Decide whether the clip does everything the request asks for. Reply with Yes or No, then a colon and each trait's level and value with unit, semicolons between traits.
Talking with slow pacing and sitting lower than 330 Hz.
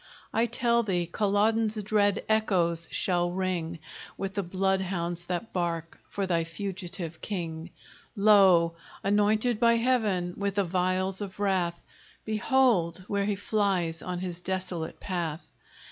Yes: slow, 130 wpm; high, 190 Hz